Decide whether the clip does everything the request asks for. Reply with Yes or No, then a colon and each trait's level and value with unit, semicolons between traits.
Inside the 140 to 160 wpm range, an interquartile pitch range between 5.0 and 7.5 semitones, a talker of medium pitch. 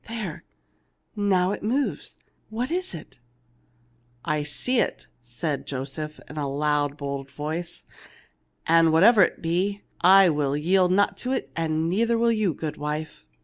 Yes: average, 150 wpm; wide, 5.5 semitones; medium, 165 Hz